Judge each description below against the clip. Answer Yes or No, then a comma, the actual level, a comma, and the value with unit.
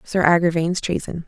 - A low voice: No, medium, 170 Hz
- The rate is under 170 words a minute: Yes, average, 140 wpm